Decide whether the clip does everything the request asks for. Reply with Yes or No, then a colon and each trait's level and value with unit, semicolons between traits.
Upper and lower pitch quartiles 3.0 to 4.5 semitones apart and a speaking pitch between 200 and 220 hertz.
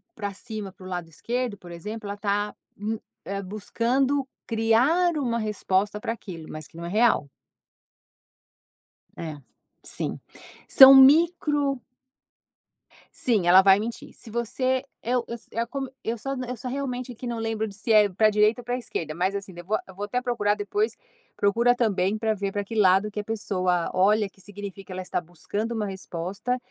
Yes: average, 3.9 semitones; high, 215 Hz